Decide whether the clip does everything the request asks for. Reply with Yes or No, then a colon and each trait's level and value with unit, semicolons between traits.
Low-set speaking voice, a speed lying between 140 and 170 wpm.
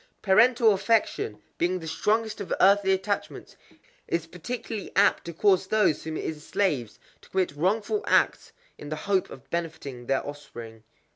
No: medium, 185 Hz; average, 150 wpm